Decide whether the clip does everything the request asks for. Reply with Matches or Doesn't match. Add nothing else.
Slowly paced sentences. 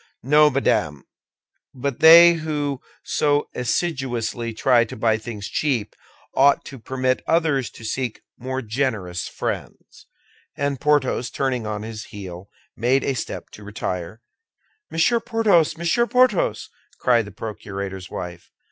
Matches